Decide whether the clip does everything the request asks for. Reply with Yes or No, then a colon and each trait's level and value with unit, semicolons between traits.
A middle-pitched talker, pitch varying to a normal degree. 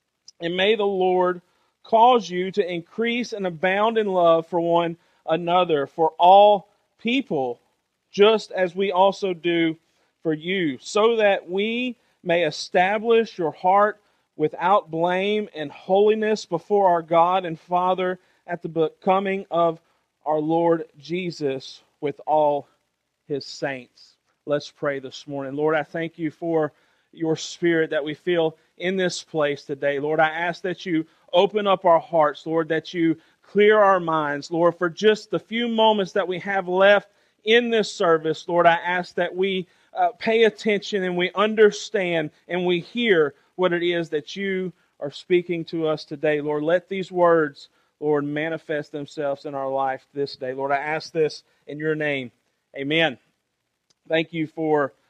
Yes: medium, 170 Hz; average, 3.8 semitones